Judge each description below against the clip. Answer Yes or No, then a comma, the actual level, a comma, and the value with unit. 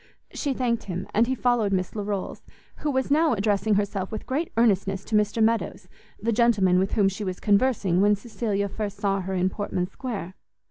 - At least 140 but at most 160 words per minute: No, average, 190 wpm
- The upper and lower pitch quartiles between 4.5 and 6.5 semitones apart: No, average, 3.2 semitones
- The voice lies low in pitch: No, high, 205 Hz